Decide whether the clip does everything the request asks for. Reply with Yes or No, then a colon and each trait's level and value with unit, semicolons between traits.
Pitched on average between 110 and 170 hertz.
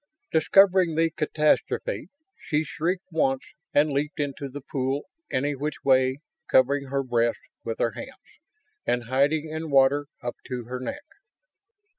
Yes: medium, 140 Hz